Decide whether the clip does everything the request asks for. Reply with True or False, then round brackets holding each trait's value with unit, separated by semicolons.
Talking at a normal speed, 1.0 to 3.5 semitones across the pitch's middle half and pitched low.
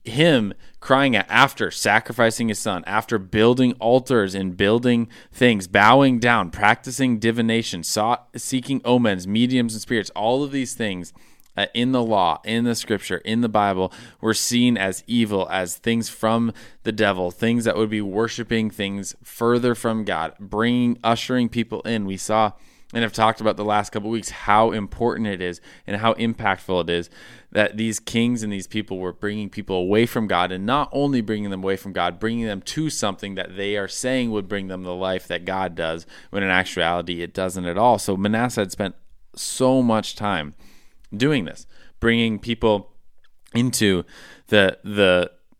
True (180 wpm; 3.2 semitones; 110 Hz)